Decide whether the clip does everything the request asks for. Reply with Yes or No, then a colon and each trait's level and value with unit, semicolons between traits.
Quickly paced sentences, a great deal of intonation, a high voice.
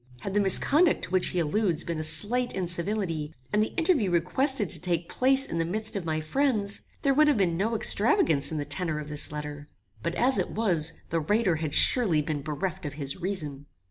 No: fast, 210 wpm; wide, 5.9 semitones; medium, 180 Hz